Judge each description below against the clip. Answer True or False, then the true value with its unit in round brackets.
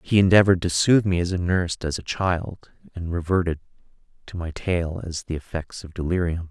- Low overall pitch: True (90 Hz)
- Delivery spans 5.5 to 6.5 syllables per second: True (5.6 syllables/s)